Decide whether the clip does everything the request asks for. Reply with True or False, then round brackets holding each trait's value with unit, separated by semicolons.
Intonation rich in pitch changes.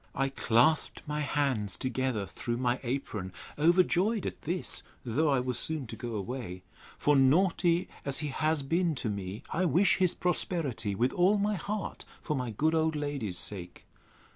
True (5.7 semitones)